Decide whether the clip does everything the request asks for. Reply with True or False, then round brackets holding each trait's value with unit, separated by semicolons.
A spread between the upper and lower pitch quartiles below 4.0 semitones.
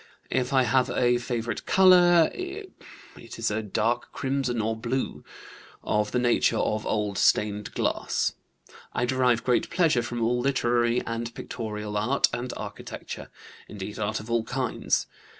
True (2.9 semitones)